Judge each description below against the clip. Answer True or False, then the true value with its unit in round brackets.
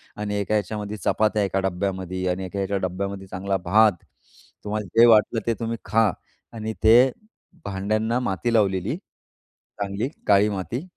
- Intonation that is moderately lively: False (2.3 semitones)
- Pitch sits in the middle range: False (105 Hz)